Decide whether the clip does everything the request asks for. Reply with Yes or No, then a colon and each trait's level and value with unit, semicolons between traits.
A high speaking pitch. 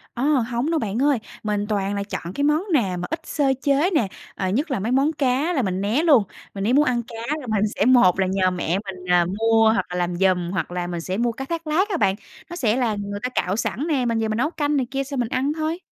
Yes: high, 230 Hz